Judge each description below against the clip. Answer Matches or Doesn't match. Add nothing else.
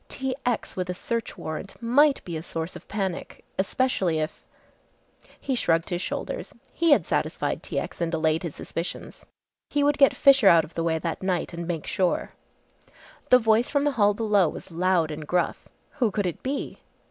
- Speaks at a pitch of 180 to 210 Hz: Matches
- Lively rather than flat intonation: Matches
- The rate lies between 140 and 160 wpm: Doesn't match